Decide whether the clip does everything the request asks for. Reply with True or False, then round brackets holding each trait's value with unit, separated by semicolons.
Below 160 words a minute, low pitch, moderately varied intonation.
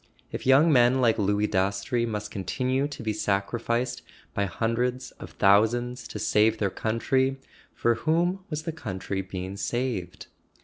True (150 wpm; 115 Hz; 4.1 semitones)